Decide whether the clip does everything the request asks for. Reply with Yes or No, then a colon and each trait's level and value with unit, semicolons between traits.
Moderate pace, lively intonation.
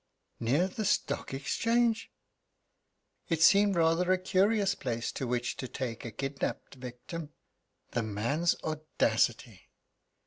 No: slow, 115 wpm; wide, 7.3 semitones